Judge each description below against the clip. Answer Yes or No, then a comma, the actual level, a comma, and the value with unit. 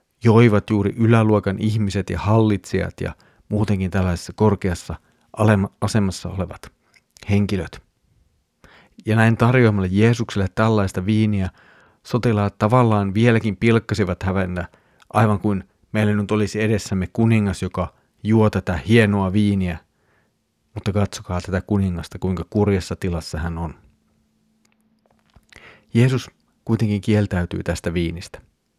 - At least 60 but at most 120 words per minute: Yes, average, 105 wpm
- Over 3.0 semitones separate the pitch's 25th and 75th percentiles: No, average, 2.7 semitones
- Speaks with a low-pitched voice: Yes, low, 105 Hz